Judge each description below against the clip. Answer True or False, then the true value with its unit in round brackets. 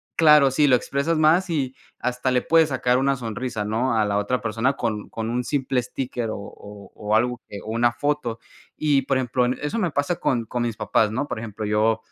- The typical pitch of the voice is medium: False (125 Hz)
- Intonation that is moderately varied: True (3.7 semitones)